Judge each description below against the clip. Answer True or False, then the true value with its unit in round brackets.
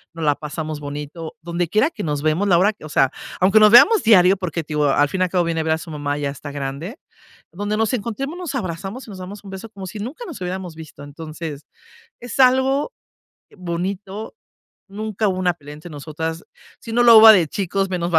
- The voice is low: False (185 Hz)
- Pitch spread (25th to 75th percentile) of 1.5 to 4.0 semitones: False (5.1 semitones)